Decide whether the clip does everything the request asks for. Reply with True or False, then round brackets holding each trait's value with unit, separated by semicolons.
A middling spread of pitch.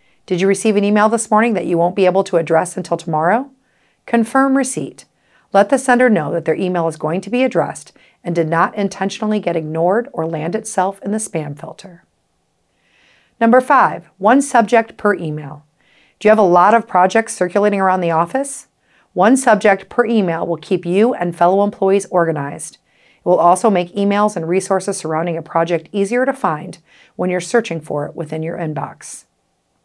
True (4.5 semitones)